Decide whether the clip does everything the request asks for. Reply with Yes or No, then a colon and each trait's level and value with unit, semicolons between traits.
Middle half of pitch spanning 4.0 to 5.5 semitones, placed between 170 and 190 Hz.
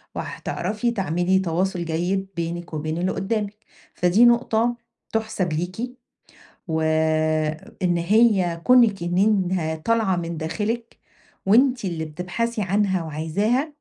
Yes: average, 4.7 semitones; medium, 185 Hz